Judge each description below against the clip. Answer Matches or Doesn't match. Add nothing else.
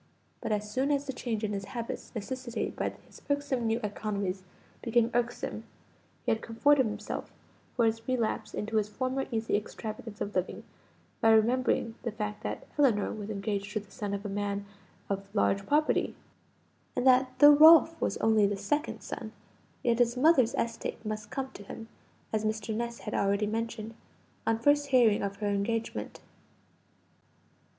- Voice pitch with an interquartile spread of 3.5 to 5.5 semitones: Doesn't match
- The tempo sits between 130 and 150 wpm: Doesn't match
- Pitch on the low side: Doesn't match